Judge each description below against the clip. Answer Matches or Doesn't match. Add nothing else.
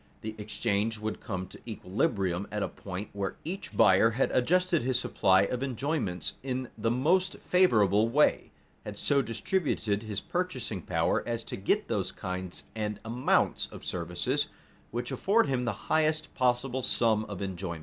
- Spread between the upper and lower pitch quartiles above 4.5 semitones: Matches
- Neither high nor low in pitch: Doesn't match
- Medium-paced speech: Matches